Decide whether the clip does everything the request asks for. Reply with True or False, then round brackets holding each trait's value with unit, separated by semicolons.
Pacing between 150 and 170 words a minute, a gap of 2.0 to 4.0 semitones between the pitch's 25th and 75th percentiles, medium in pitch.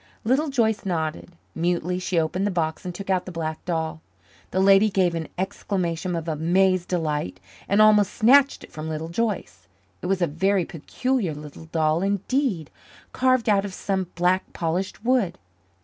True (165 wpm; 3.6 semitones; 180 Hz)